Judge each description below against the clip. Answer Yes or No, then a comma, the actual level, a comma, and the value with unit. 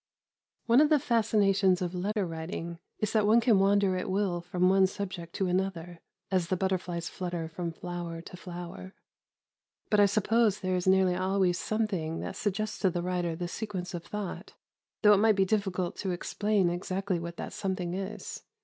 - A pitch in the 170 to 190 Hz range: Yes, medium, 185 Hz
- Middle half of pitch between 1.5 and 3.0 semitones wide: Yes, narrow, 2.6 semitones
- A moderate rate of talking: Yes, average, 180 wpm